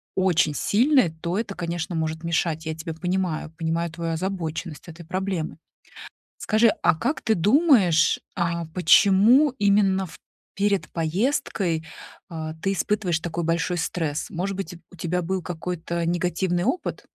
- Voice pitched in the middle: Yes, medium, 175 Hz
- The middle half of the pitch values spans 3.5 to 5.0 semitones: No, average, 3.1 semitones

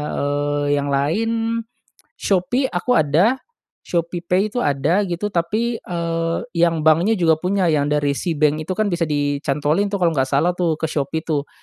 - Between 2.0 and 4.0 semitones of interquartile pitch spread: No, average, 4.4 semitones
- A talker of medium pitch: Yes, medium, 165 Hz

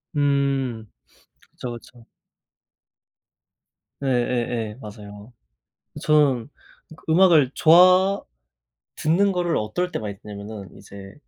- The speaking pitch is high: No, low, 125 Hz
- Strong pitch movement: Yes, wide, 6.9 semitones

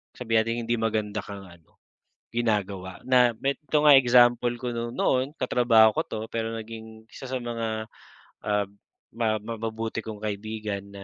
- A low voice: Yes, low, 115 Hz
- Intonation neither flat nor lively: No, narrow, 2.0 semitones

